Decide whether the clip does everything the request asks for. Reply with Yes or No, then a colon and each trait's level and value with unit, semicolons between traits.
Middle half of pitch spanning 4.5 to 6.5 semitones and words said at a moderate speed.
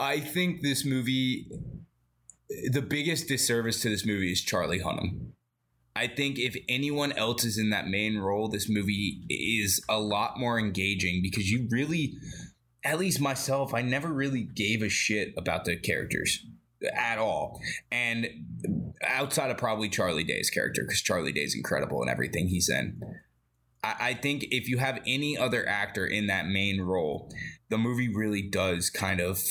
Yes: average, 5.2 semitones; average, 165 wpm